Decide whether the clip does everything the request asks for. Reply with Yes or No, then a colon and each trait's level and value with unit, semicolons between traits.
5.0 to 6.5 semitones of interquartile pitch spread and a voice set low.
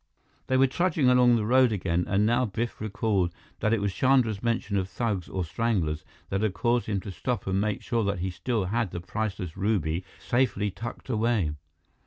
No: average, 3.9 semitones; low, 105 Hz